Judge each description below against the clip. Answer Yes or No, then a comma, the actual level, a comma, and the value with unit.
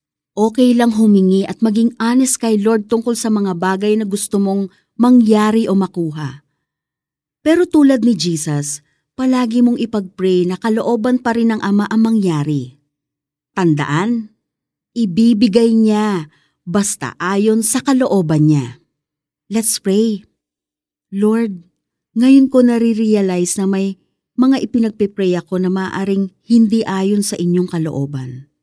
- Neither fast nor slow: Yes, average, 125 wpm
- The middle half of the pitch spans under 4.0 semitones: No, wide, 5.6 semitones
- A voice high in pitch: Yes, high, 200 Hz